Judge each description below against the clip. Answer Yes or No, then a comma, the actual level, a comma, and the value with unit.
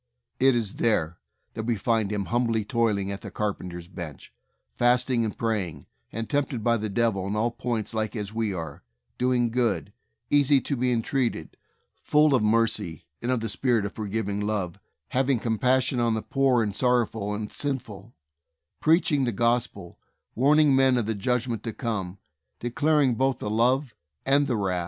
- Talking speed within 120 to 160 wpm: No, average, 175 wpm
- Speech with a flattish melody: No, average, 3.4 semitones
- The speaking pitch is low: Yes, low, 115 Hz